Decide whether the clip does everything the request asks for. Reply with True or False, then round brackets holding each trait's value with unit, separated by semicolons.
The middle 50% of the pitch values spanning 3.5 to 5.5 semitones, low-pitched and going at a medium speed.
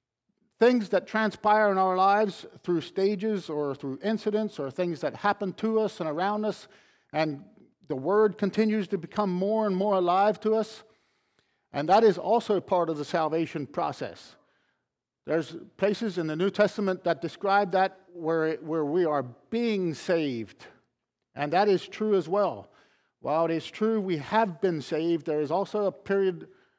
False (4.4 semitones; 190 Hz; 170 wpm)